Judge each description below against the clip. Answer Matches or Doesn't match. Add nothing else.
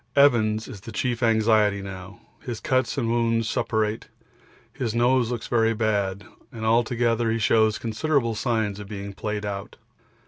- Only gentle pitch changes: Matches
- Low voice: Matches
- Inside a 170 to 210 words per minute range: Doesn't match